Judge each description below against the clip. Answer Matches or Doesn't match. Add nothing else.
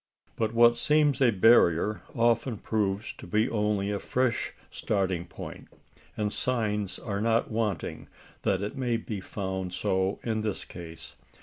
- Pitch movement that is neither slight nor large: Matches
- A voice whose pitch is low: Matches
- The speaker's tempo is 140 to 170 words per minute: Matches